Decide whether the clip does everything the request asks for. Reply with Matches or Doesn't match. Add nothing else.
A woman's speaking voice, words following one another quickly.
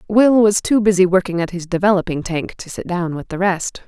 Matches